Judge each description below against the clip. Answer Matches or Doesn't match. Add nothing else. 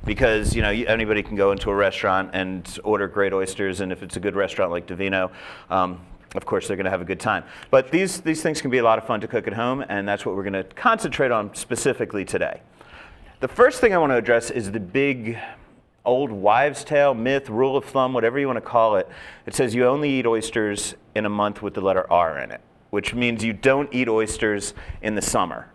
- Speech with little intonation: Doesn't match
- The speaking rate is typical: Doesn't match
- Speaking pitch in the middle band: Doesn't match